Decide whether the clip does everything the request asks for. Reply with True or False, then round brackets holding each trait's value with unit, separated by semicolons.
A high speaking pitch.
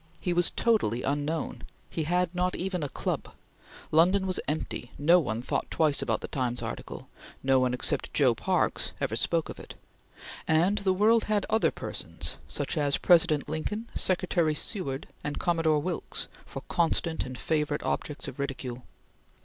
False (160 Hz)